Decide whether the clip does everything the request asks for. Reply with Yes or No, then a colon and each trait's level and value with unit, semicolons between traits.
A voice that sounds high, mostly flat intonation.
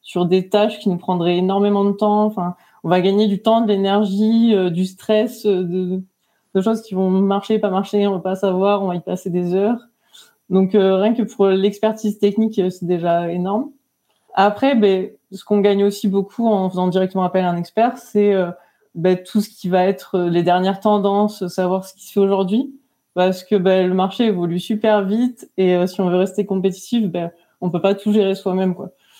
Yes: high, 195 Hz; narrow, 2.3 semitones